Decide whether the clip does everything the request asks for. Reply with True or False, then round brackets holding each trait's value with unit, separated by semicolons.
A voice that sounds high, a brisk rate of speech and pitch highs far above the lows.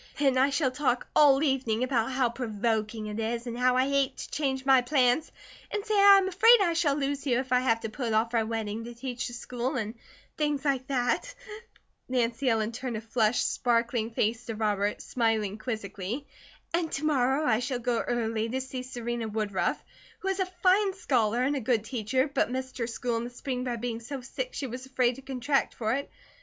False (250 Hz; 210 wpm; 3.1 semitones)